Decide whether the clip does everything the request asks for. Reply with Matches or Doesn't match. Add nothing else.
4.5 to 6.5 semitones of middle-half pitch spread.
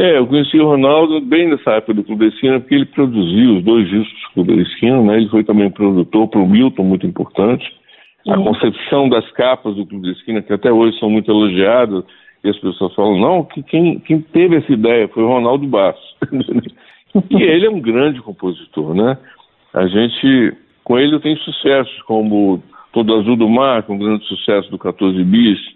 Matches